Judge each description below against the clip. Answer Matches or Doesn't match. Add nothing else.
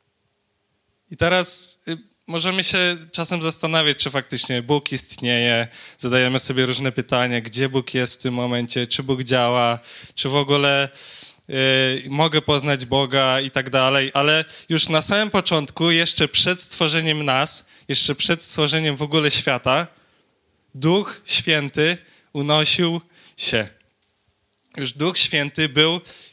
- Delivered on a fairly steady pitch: Doesn't match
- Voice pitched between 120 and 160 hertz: Matches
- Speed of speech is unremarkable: Matches